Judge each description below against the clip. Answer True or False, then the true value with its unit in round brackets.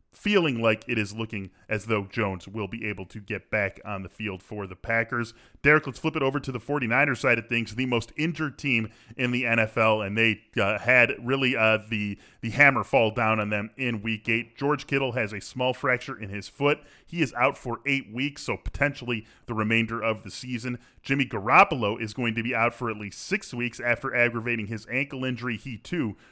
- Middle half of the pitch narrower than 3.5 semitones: True (3.0 semitones)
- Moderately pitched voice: False (115 Hz)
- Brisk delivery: True (215 wpm)